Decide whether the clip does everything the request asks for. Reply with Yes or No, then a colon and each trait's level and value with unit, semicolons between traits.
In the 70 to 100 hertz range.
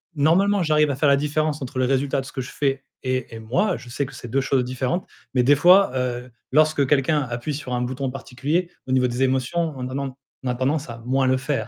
No: low, 135 Hz